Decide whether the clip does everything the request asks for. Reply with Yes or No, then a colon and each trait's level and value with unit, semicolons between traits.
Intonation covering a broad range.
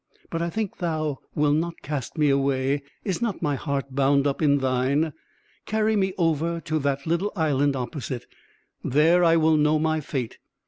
No: average, 3.2 semitones